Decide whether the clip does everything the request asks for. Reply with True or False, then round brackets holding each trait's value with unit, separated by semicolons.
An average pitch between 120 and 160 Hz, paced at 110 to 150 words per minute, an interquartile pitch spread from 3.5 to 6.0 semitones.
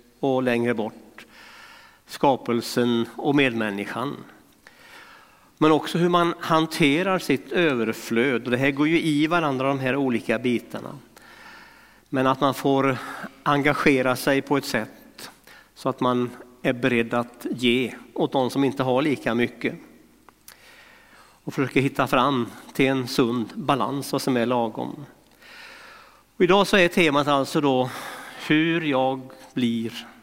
True (135 Hz; 135 wpm; 4.0 semitones)